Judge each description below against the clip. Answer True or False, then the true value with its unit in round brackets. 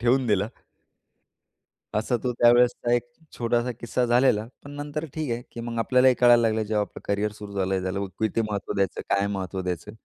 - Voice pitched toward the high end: False (115 Hz)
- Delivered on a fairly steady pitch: False (3.2 semitones)